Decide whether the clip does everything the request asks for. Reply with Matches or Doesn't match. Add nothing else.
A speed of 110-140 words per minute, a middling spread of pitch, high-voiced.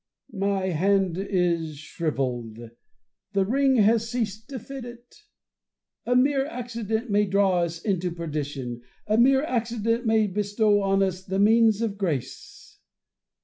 Matches